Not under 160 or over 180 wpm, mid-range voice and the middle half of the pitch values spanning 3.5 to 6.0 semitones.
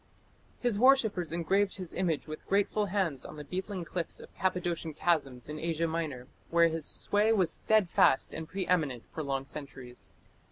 Yes: average, 165 wpm; medium, 170 Hz; average, 4.0 semitones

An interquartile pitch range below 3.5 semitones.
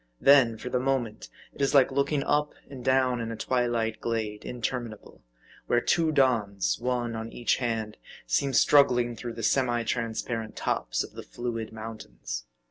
Yes: narrow, 2.5 semitones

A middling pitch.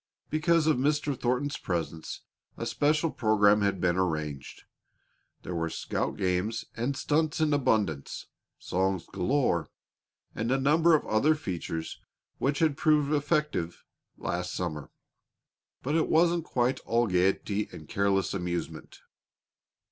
No: low, 115 Hz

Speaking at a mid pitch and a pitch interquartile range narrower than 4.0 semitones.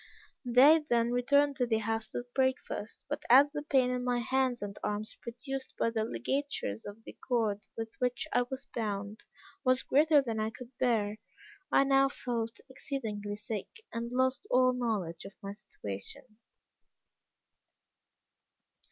No: high, 240 Hz; average, 3.4 semitones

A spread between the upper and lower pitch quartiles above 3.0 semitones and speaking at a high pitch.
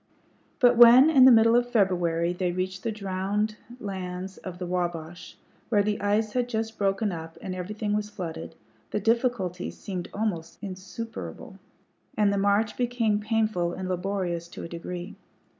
Yes: average, 3.5 semitones; high, 200 Hz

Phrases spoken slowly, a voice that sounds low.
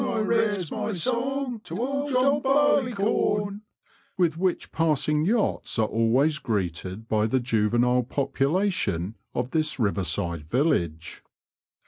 No: slow, 125 wpm; medium, 155 Hz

